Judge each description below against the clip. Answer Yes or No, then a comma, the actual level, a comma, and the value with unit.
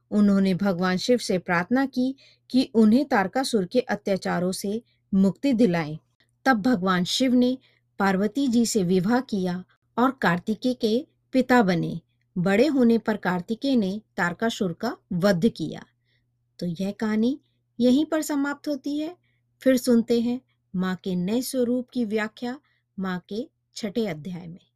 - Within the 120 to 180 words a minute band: Yes, average, 145 wpm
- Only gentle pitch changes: No, average, 5.3 semitones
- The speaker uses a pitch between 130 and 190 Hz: No, high, 215 Hz